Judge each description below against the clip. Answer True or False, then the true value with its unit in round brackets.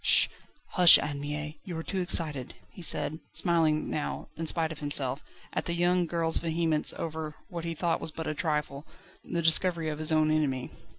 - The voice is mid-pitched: True (160 Hz)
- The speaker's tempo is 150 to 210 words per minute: True (190 wpm)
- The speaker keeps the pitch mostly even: True (2.0 semitones)